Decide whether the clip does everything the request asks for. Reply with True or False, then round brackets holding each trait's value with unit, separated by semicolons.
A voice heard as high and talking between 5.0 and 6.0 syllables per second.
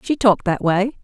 True (210 Hz; 5.4 syllables/s)